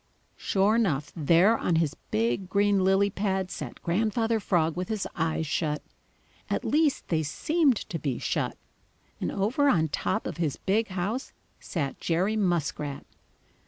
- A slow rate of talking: No, average, 150 wpm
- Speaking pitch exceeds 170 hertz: Yes, medium, 185 Hz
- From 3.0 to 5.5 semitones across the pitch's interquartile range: Yes, average, 4.9 semitones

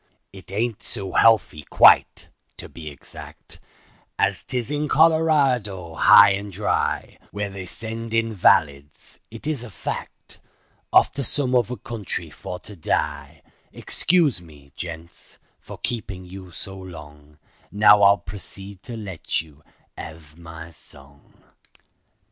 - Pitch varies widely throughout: Yes, wide, 5.7 semitones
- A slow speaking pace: Yes, slow, 125 wpm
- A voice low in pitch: Yes, low, 100 Hz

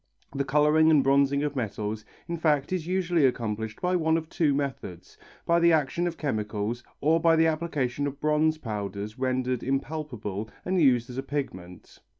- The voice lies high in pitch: No, medium, 140 Hz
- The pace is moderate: Yes, average, 170 wpm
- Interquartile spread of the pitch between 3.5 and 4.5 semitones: No, average, 5.0 semitones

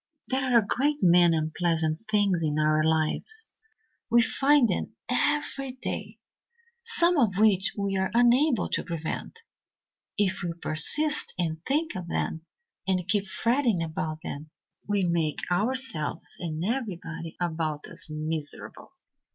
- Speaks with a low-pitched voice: No, medium, 185 Hz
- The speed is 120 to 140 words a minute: Yes, slow, 135 wpm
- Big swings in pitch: Yes, wide, 7.6 semitones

